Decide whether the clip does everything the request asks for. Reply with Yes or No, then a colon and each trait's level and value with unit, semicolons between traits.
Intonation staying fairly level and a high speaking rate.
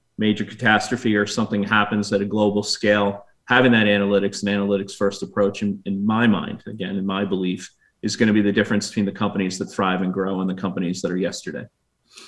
Yes: narrow, 1.4 semitones; fast, 210 wpm